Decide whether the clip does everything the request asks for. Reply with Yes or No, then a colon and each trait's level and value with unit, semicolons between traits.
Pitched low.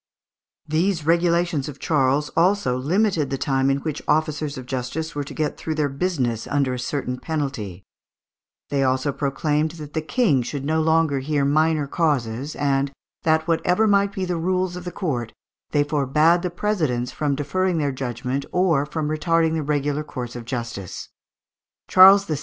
No: medium, 150 Hz